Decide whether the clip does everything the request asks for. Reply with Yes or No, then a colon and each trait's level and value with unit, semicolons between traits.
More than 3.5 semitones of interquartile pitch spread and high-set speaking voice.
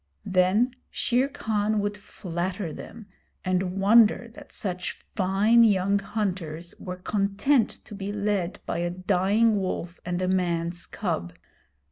No: average, 2.7 semitones; high, 195 Hz